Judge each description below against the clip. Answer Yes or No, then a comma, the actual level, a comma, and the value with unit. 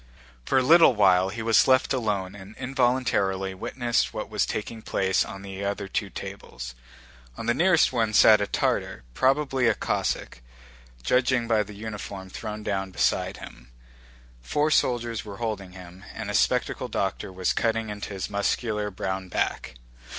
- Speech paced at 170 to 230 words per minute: No, average, 160 wpm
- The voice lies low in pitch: Yes, low, 105 Hz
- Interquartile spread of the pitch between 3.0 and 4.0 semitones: Yes, average, 3.7 semitones